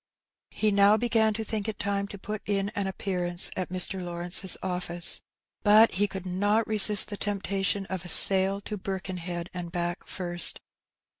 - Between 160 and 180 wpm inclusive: Yes, average, 170 wpm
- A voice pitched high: Yes, high, 195 Hz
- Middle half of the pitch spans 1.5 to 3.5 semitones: Yes, narrow, 2.4 semitones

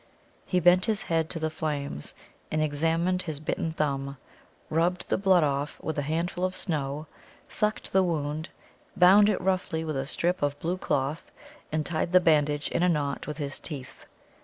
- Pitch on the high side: No, medium, 160 Hz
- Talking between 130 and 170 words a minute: No, average, 180 wpm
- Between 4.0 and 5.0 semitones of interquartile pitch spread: No, average, 3.5 semitones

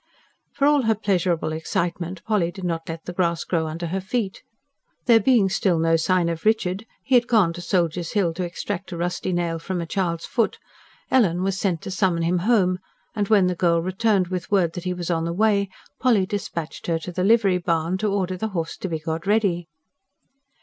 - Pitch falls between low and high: Yes, medium, 180 Hz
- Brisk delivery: Yes, fast, 210 wpm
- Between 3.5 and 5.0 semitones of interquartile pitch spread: No, average, 3.0 semitones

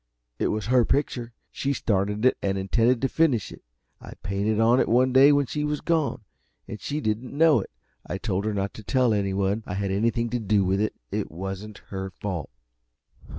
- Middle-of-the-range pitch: No, low, 110 Hz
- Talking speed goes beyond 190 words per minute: Yes, average, 200 wpm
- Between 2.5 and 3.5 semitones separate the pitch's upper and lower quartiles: No, average, 4.6 semitones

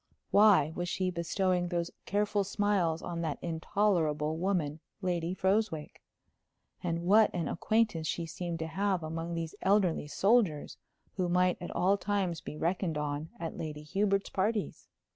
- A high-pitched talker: No, medium, 175 Hz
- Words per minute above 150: No, average, 145 wpm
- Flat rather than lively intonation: No, average, 3.5 semitones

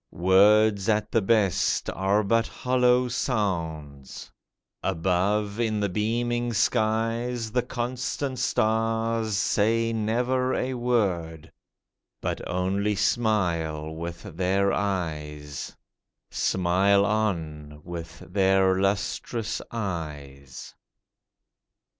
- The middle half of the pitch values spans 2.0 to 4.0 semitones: No, average, 4.6 semitones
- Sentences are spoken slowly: Yes, slow, 85 wpm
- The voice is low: Yes, low, 100 Hz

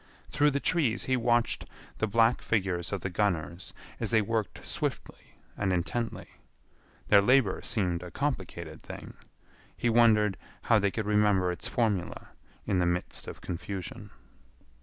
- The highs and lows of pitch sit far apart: No, average, 4.3 semitones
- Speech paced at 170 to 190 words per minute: No, average, 145 wpm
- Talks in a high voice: No, low, 105 Hz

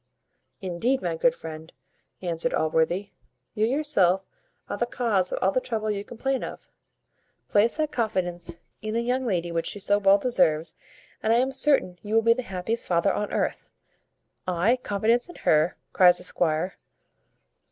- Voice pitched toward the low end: No, high, 205 Hz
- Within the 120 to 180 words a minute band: Yes, average, 165 wpm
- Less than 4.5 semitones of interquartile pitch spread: No, average, 5.1 semitones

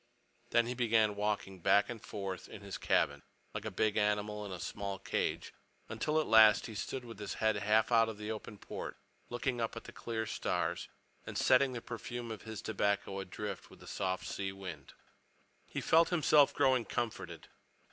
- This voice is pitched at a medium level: No, low, 105 Hz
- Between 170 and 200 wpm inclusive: Yes, average, 185 wpm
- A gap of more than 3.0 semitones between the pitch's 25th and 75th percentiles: No, narrow, 2.6 semitones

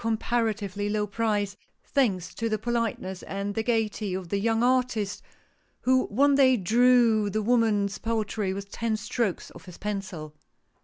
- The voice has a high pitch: Yes, high, 215 Hz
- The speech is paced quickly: No, average, 150 wpm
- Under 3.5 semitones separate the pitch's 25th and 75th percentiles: Yes, narrow, 2.6 semitones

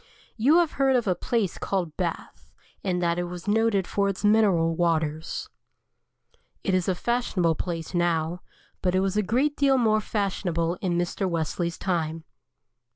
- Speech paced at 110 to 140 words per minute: No, average, 160 wpm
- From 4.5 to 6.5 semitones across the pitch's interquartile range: No, average, 4.0 semitones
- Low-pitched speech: No, medium, 185 Hz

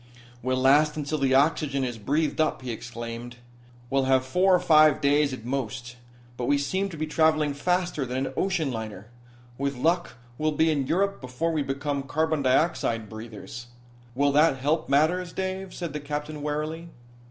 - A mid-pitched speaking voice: Yes, medium, 145 Hz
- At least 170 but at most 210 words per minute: Yes, average, 175 wpm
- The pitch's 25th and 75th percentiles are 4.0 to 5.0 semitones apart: No, average, 3.4 semitones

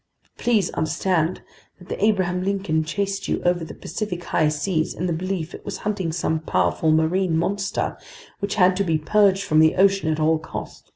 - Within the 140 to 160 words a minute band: No, average, 190 wpm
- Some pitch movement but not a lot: Yes, average, 3.6 semitones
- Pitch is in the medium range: Yes, medium, 180 Hz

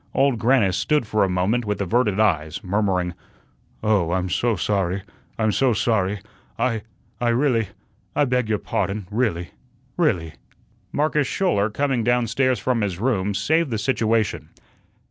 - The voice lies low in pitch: Yes, low, 110 Hz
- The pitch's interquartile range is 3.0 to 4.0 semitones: No, average, 4.5 semitones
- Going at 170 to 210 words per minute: No, average, 145 wpm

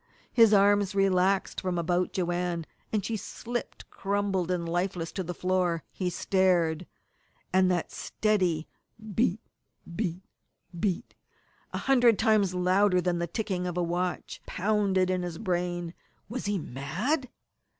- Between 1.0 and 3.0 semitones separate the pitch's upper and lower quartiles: Yes, narrow, 2.5 semitones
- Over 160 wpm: No, slow, 135 wpm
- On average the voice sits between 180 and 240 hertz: Yes, medium, 185 Hz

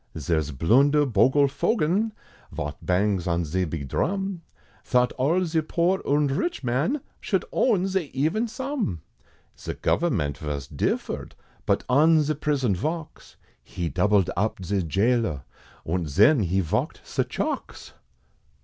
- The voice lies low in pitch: Yes, low, 125 Hz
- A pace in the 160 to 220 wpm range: No, slow, 135 wpm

